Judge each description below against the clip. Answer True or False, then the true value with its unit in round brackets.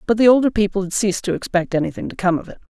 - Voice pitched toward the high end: True (200 Hz)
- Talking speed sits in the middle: False (290 wpm)